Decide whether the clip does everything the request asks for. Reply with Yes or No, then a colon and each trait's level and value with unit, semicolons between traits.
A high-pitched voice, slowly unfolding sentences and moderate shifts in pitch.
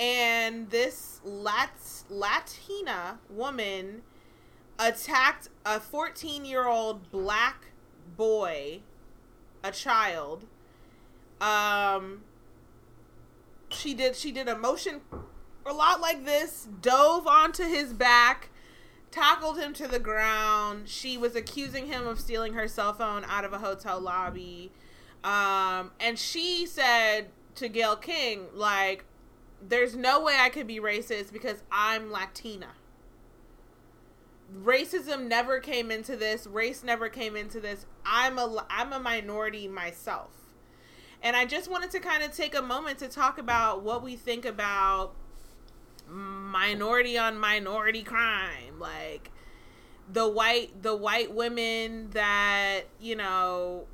Yes: high, 225 Hz; slow, 120 wpm; average, 3.9 semitones